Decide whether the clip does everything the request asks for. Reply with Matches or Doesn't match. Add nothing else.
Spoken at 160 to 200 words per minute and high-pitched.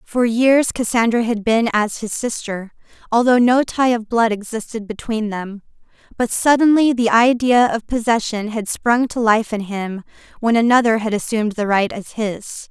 Matches